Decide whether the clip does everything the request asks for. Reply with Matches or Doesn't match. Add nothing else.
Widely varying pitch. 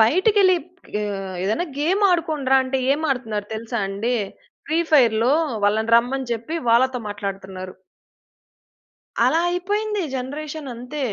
Matches